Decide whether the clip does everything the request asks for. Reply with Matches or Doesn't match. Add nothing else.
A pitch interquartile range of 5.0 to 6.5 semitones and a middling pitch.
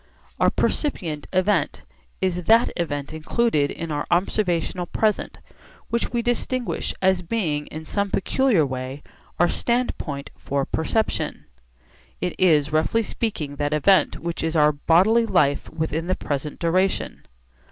Matches